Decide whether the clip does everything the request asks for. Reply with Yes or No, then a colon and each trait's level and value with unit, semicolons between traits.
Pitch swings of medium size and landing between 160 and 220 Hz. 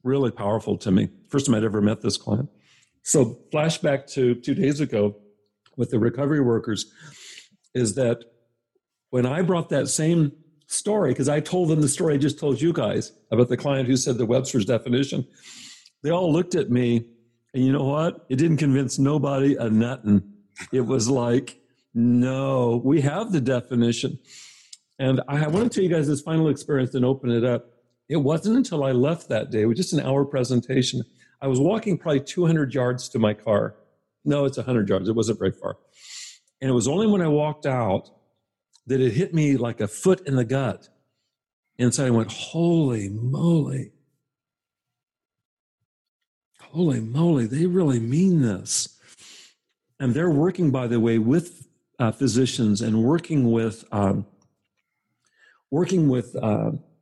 No: average, 4.1 semitones; low, 135 Hz